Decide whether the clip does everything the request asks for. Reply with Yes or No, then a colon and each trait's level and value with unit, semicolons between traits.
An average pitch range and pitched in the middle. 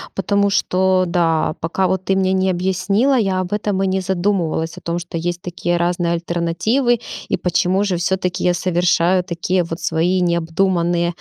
No: narrow, 1.9 semitones; medium, 180 Hz